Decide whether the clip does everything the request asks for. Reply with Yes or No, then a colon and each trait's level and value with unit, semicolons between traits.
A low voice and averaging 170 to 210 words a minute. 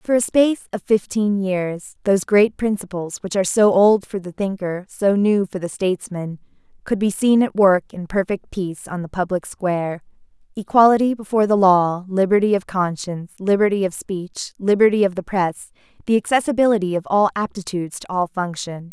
No: high, 195 Hz; average, 175 wpm